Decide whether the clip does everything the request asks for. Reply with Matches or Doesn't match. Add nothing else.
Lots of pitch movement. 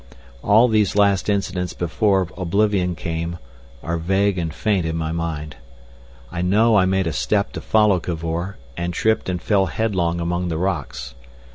Doesn't match